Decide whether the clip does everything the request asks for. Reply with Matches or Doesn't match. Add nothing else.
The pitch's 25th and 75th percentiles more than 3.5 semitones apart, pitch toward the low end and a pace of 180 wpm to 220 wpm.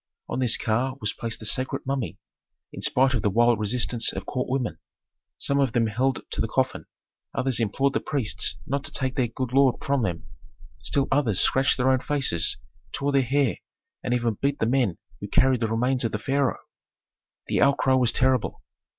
Doesn't match